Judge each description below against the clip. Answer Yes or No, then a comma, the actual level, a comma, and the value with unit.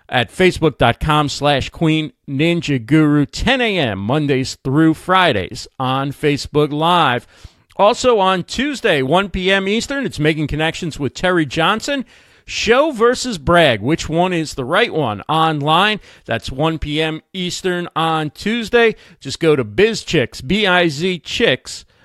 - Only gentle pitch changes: No, average, 4.3 semitones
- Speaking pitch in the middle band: Yes, medium, 160 Hz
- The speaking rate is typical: No, slow, 130 wpm